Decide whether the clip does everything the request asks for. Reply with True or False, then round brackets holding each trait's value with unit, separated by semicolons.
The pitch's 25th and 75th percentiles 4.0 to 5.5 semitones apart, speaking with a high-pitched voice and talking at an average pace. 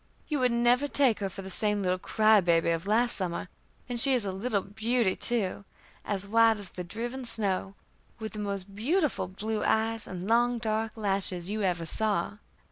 False (3.4 semitones; 215 Hz; 190 wpm)